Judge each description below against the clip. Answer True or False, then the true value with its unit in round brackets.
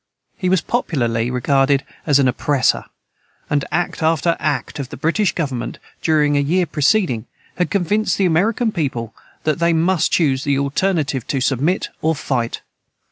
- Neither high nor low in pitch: True (150 Hz)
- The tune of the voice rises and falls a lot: False (4.6 semitones)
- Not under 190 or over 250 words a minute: False (155 wpm)